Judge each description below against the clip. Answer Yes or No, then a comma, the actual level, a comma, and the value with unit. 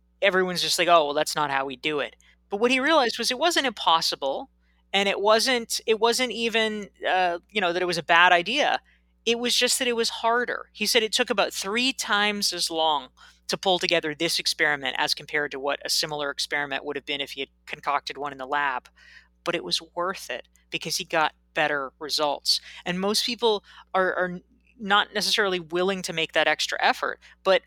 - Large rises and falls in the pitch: Yes, wide, 6.3 semitones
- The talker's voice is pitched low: No, medium, 180 Hz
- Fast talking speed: Yes, fast, 210 wpm